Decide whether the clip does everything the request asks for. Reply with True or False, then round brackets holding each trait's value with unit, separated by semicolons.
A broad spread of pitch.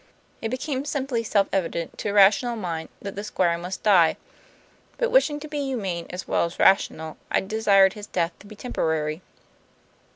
True (5.7 semitones)